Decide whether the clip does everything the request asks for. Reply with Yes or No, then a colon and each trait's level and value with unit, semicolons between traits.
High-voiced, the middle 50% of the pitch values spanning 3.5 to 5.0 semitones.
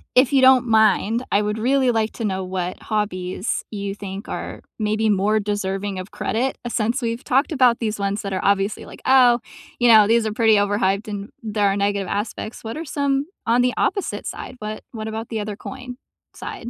No: high, 215 Hz; average, 3.0 semitones